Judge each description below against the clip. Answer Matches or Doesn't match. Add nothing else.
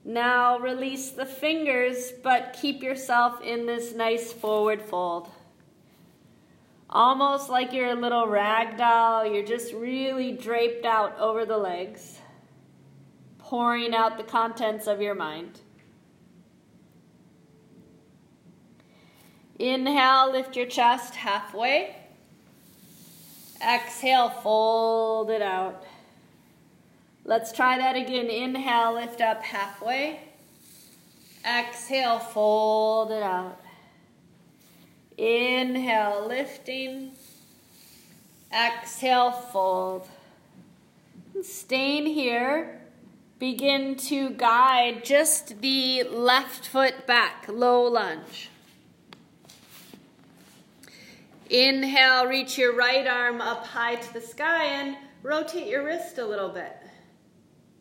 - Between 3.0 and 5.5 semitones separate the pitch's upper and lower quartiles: Doesn't match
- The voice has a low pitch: Doesn't match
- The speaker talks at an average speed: Doesn't match